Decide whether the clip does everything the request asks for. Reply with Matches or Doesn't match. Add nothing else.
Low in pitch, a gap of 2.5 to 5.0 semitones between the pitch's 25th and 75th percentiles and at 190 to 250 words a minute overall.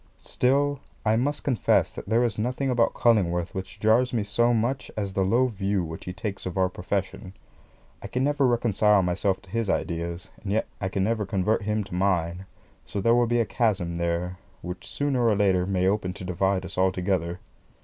Matches